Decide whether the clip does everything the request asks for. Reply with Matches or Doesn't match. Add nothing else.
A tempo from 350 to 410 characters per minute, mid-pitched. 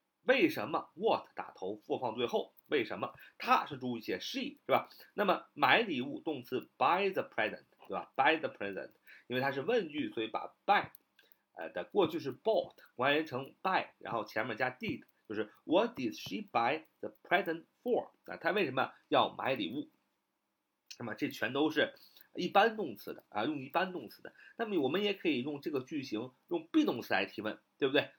Doesn't match